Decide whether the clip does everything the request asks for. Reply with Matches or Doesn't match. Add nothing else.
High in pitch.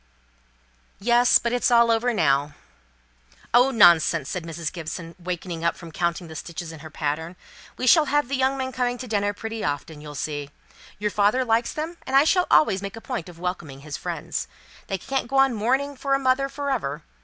Matches